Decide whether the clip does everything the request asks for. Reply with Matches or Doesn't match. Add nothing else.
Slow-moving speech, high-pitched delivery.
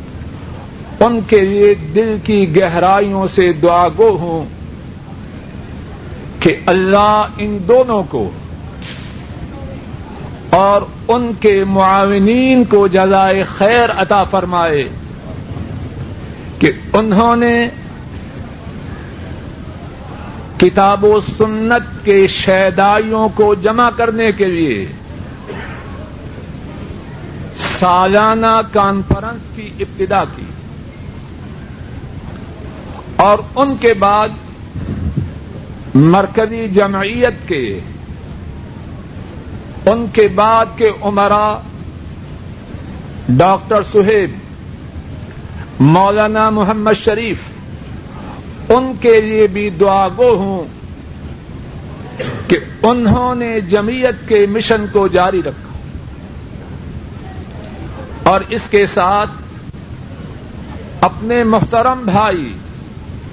Matches